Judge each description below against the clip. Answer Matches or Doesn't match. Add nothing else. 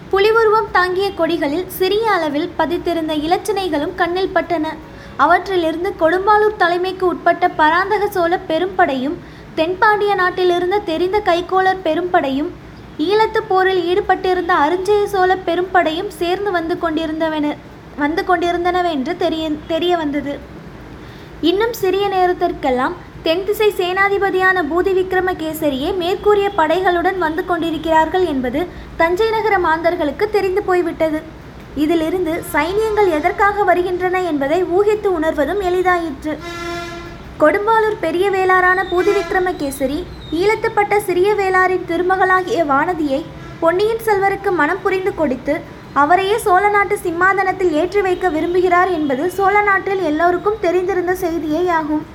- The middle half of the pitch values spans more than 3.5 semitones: Doesn't match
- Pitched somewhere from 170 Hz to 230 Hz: Doesn't match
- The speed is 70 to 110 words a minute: Matches